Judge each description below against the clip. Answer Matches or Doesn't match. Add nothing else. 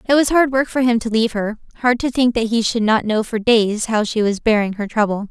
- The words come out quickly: Matches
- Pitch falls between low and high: Doesn't match